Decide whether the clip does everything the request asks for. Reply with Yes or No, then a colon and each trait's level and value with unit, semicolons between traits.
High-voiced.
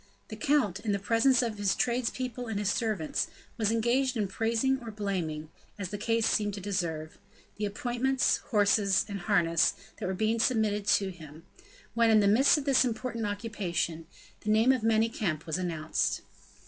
Yes: high, 215 Hz